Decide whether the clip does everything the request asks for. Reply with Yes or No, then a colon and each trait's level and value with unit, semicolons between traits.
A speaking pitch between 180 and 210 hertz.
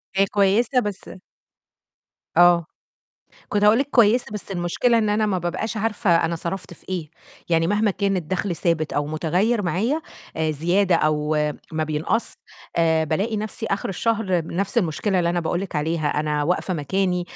Yes: medium, 185 Hz